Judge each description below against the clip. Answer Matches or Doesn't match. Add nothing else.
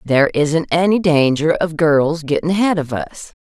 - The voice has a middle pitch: Matches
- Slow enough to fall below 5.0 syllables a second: Matches